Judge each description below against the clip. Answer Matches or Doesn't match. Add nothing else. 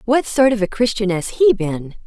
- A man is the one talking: Doesn't match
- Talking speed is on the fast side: Matches